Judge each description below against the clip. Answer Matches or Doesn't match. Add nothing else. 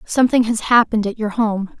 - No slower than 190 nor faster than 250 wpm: Matches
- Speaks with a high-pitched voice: Matches